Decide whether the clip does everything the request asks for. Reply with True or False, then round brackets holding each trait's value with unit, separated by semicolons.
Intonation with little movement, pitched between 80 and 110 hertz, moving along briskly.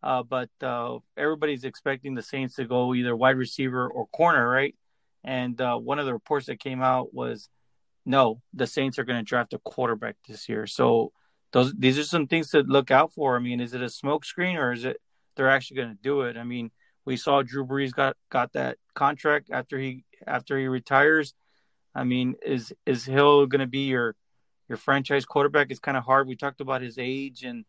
False (1.9 semitones; 130 Hz; 210 wpm)